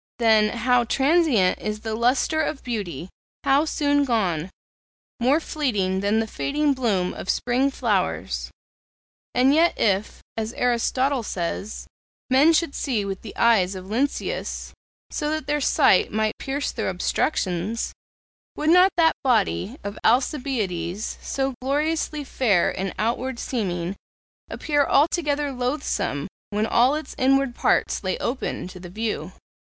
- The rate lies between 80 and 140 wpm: Yes, slow, 135 wpm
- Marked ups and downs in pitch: Yes, wide, 5.7 semitones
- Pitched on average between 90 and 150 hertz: No, high, 240 Hz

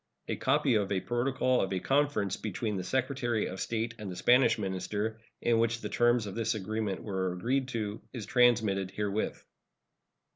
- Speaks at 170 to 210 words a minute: Yes, average, 175 wpm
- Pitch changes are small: No, average, 3.6 semitones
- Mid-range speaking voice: No, low, 110 Hz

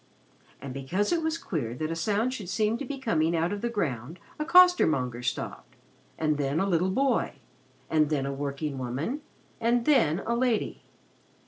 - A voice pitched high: No, medium, 170 Hz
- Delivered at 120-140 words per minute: No, average, 170 wpm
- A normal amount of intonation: No, wide, 8.8 semitones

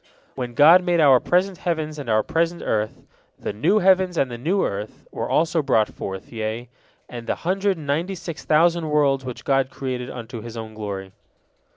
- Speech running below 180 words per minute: No, average, 190 wpm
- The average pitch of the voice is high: No, medium, 140 Hz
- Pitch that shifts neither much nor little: No, wide, 6.5 semitones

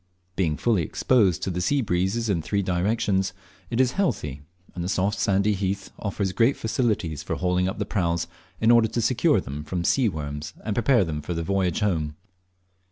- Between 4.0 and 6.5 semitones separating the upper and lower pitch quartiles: Yes, average, 4.4 semitones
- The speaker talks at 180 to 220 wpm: Yes, average, 190 wpm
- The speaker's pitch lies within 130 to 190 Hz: No, very low, 95 Hz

